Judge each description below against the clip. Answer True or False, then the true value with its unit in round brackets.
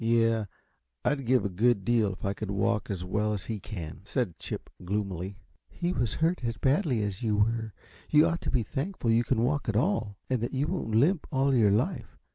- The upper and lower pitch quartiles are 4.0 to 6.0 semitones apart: True (4.5 semitones)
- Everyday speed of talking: False (215 wpm)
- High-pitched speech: False (115 Hz)